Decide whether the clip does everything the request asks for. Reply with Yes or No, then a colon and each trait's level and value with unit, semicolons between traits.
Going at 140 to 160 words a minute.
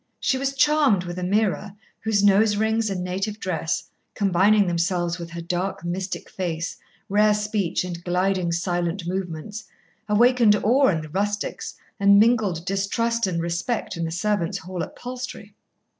Yes: average, 150 wpm